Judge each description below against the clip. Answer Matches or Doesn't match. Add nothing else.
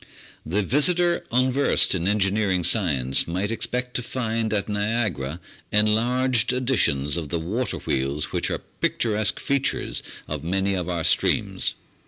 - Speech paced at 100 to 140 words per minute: Matches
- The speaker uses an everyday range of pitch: Doesn't match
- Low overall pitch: Matches